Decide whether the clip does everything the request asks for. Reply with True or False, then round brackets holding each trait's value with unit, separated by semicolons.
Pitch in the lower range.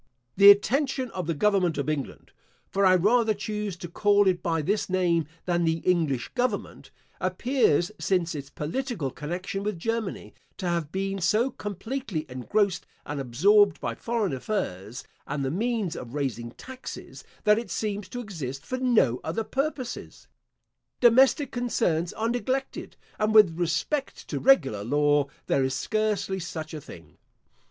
False (190 Hz)